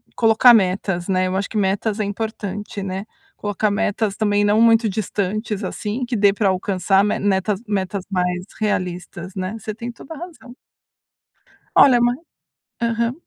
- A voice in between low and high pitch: No, high, 205 Hz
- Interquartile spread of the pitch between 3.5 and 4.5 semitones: No, average, 2.7 semitones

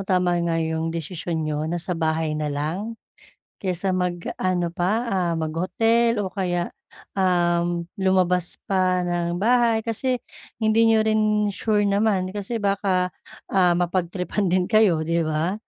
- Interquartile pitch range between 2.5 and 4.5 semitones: Yes, average, 3.1 semitones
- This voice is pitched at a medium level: Yes, medium, 180 Hz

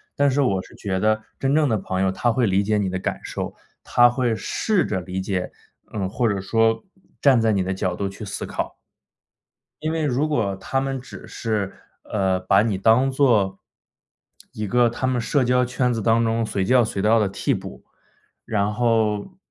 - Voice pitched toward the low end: Yes, low, 110 Hz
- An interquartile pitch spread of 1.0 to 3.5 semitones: No, average, 4.3 semitones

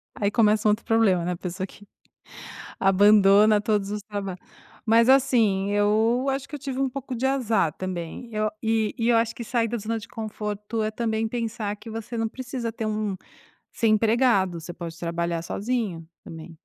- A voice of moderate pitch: No, high, 215 Hz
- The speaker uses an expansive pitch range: No, average, 2.7 semitones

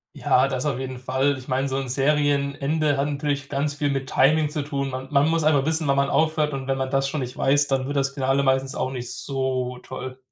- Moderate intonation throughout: No, narrow, 1.6 semitones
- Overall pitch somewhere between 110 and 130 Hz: No, medium, 140 Hz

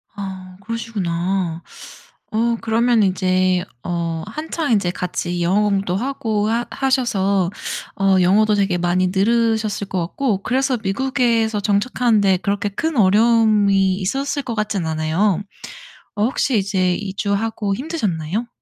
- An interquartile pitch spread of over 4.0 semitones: No, average, 3.6 semitones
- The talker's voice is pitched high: Yes, high, 205 Hz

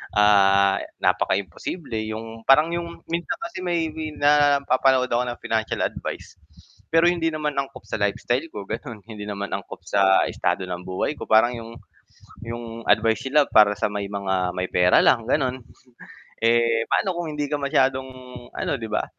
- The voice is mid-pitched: No, low, 115 Hz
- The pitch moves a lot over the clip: Yes, wide, 5.9 semitones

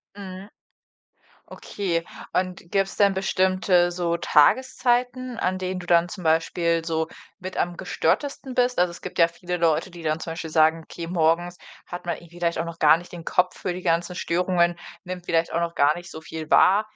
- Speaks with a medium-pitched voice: Yes, medium, 175 Hz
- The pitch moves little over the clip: Yes, narrow, 1.9 semitones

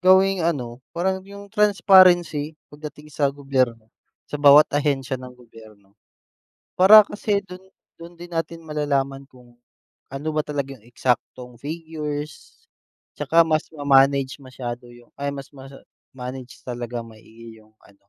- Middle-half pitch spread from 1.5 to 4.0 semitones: No, average, 4.8 semitones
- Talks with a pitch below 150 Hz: Yes, medium, 140 Hz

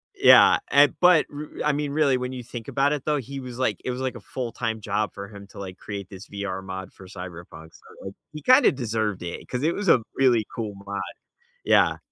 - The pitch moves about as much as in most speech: No, wide, 5.8 semitones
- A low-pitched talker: Yes, low, 115 Hz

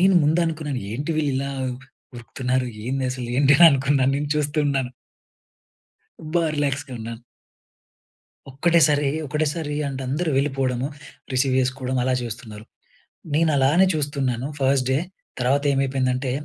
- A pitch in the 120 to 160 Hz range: Yes, low, 135 Hz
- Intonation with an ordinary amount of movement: No, narrow, 2.3 semitones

